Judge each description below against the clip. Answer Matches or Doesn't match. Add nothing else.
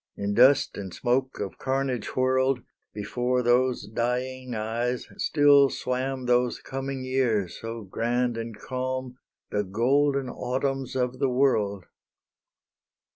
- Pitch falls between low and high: Doesn't match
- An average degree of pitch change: Doesn't match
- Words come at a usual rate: Doesn't match